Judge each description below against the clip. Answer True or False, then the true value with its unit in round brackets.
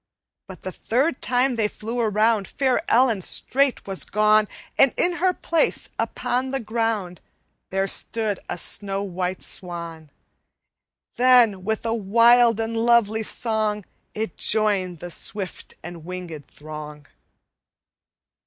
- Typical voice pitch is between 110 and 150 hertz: False (215 Hz)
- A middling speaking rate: False (125 wpm)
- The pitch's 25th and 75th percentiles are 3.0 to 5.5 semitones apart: True (4.1 semitones)